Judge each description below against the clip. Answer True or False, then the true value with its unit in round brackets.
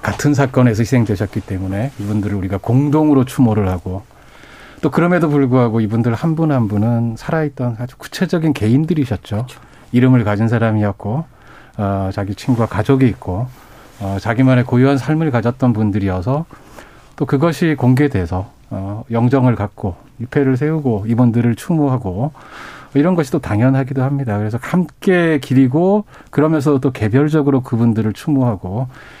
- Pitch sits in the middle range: False (125 Hz)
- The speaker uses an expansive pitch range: False (4.9 semitones)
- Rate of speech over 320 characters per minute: True (350 characters per minute)